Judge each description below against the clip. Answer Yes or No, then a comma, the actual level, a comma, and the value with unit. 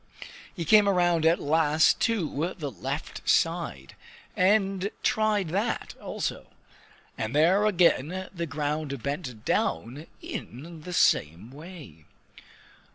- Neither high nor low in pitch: Yes, medium, 160 Hz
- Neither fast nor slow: No, slow, 110 wpm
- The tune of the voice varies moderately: Yes, average, 4.9 semitones